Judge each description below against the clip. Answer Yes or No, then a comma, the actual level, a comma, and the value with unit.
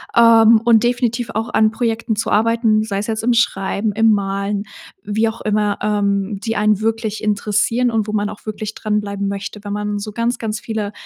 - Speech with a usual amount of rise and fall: No, narrow, 1.6 semitones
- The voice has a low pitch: No, high, 215 Hz